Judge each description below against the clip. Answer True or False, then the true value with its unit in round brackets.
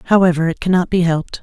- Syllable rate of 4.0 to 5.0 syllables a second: False (7.3 syllables/s)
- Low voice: False (175 Hz)